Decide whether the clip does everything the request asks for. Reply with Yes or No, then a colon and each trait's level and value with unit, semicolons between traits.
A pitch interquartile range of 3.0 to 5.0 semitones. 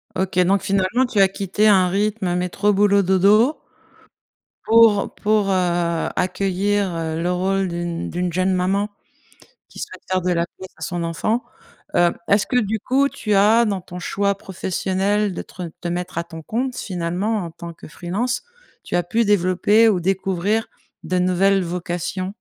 No: narrow, 2.6 semitones